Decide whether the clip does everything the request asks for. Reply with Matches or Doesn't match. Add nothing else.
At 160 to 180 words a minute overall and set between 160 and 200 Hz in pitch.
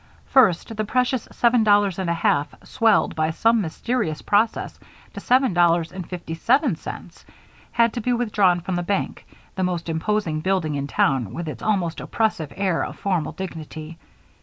Matches